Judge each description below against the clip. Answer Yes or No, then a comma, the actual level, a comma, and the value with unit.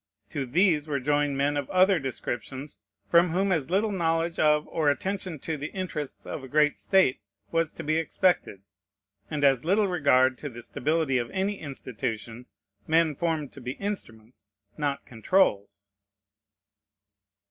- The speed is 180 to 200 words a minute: No, average, 150 wpm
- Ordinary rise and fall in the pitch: Yes, average, 4.5 semitones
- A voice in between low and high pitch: Yes, medium, 150 Hz